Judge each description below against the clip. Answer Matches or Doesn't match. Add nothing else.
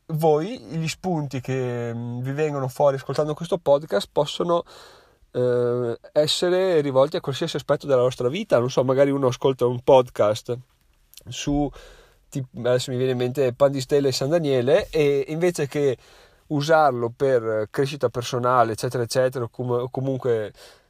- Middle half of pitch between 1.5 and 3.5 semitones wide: Matches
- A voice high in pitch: Doesn't match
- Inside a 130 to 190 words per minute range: Matches